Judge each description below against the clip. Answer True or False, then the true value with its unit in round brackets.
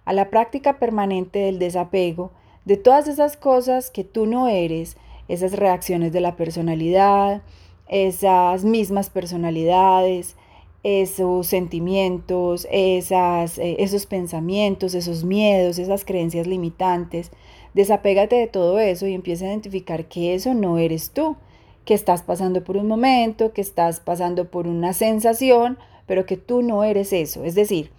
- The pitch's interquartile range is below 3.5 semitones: True (2.6 semitones)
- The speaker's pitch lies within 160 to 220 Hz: True (185 Hz)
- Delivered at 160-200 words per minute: False (140 wpm)